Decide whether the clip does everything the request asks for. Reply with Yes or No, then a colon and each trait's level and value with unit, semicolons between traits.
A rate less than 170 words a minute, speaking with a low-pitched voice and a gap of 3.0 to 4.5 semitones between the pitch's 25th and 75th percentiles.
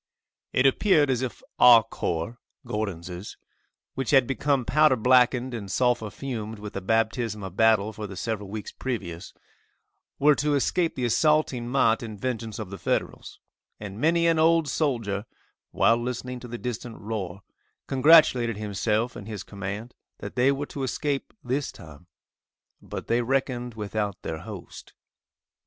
Yes: average, 150 wpm; low, 120 Hz; average, 4.0 semitones